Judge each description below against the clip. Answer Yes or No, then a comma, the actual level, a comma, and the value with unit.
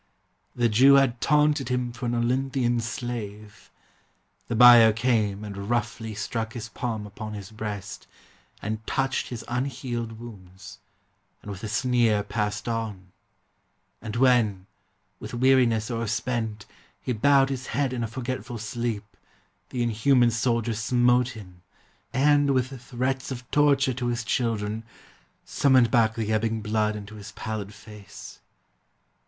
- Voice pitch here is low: Yes, low, 115 Hz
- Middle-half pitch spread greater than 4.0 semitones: No, average, 2.8 semitones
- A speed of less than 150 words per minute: Yes, slow, 135 wpm